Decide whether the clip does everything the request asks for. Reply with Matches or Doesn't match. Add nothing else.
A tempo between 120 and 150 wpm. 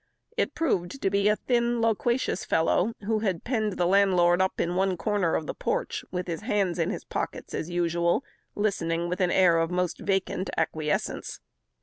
Doesn't match